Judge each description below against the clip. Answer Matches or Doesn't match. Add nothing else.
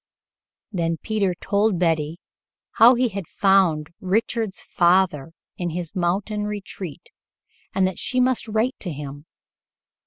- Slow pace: Matches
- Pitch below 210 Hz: Matches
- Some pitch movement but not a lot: Matches